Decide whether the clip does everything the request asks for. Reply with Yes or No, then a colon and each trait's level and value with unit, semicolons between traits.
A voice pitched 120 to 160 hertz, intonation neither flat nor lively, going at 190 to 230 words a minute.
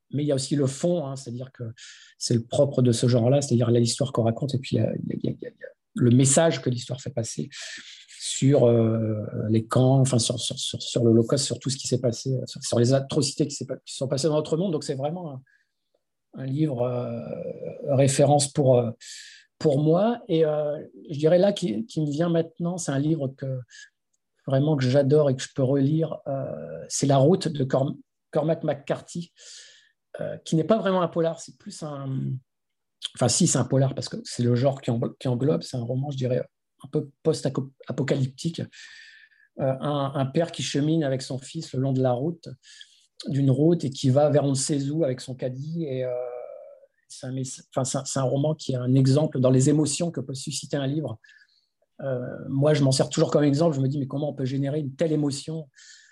Yes: medium, 140 Hz; average, 3.5 semitones; average, 210 wpm